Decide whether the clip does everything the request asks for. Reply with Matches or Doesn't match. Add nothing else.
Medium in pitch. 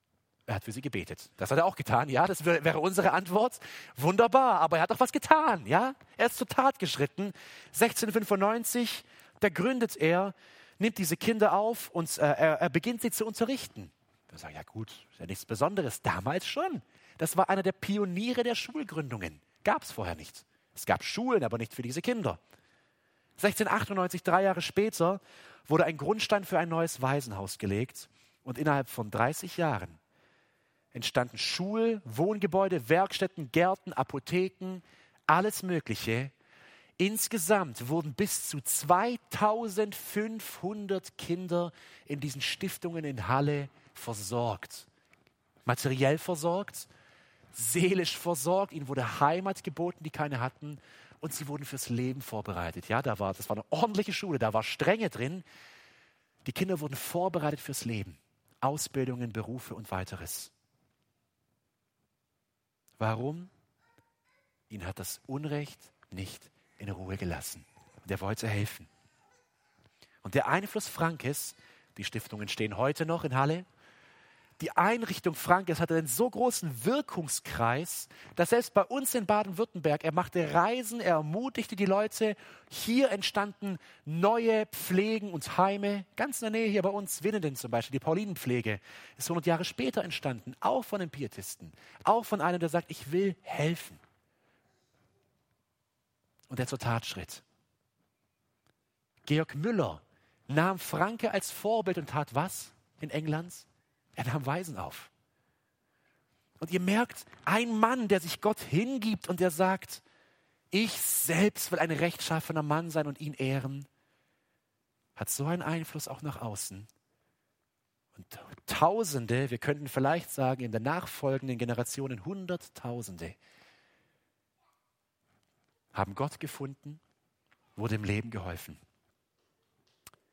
Matches